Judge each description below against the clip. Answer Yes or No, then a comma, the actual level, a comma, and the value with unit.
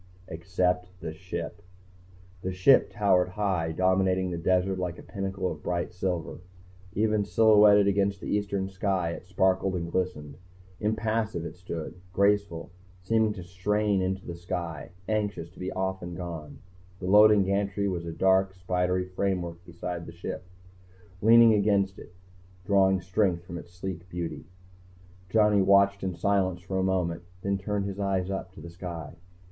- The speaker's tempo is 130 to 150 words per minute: No, average, 160 wpm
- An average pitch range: No, narrow, 2.1 semitones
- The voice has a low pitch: Yes, very low, 95 Hz